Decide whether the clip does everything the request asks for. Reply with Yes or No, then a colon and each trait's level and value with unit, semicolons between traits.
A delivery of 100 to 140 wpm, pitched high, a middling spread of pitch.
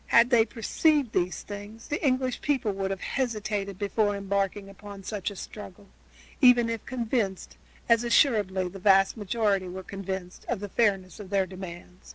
No: average, 165 wpm; high, 205 Hz; average, 3.1 semitones